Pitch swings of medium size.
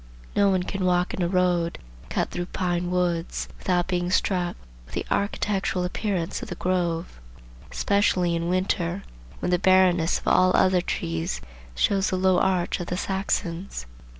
No: narrow, 1.4 semitones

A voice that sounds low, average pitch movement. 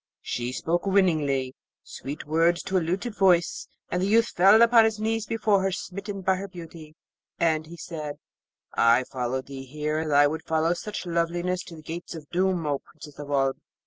No: medium, 170 Hz; average, 4.2 semitones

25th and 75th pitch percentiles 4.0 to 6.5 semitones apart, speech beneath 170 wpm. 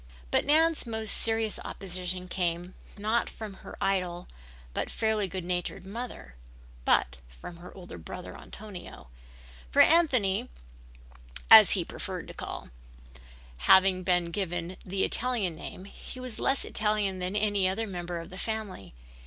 No: average, 3.6 semitones; average, 145 wpm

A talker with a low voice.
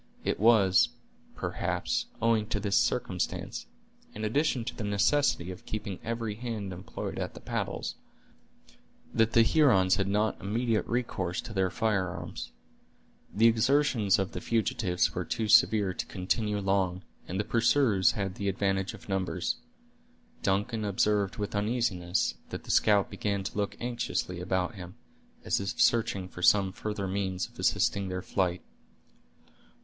Yes: low, 100 Hz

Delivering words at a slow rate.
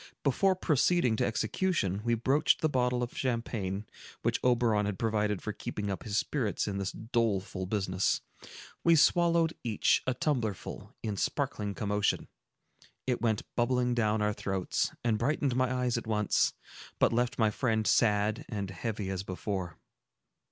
No: average, 150 wpm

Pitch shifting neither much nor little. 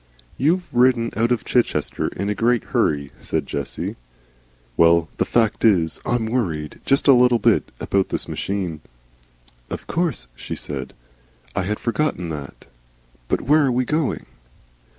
No: wide, 6.8 semitones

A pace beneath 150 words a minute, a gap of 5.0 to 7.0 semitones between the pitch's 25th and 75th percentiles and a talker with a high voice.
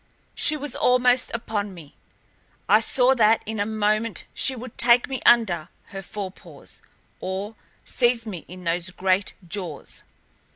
No: average, 140 wpm; average, 4.1 semitones; high, 215 Hz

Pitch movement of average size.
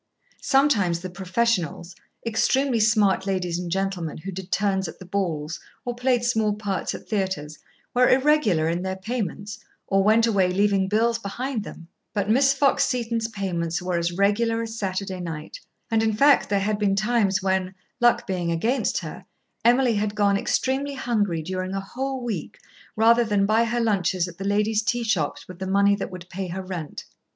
Yes: average, 3.7 semitones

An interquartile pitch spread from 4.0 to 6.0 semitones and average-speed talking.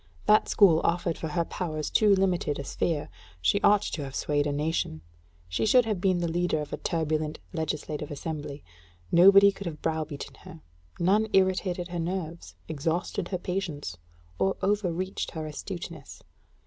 No: average, 3.6 semitones; average, 160 wpm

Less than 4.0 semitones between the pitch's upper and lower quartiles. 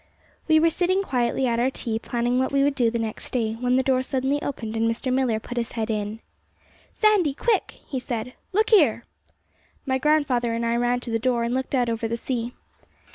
Yes: average, 2.8 semitones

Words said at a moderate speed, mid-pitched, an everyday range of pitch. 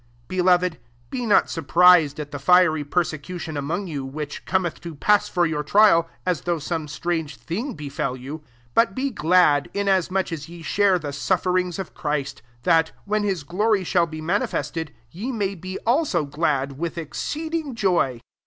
Yes: average, 170 wpm; medium, 170 Hz; average, 4.1 semitones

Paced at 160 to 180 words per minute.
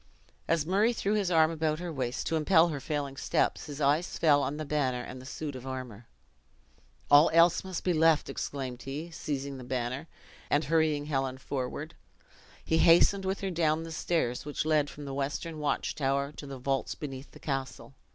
No: average, 190 wpm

